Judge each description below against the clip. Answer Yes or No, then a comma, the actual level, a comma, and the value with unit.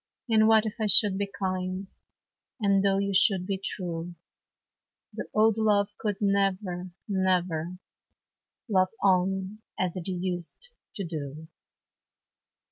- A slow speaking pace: Yes, slow, 125 wpm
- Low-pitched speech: No, high, 190 Hz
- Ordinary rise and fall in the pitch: No, narrow, 1.9 semitones